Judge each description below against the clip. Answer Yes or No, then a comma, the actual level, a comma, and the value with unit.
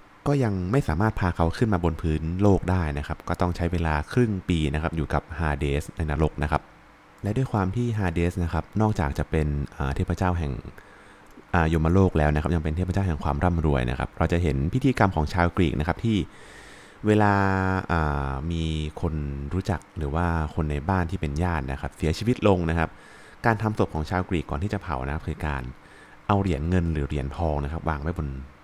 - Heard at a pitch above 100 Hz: No, very low, 85 Hz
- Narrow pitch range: No, average, 4.1 semitones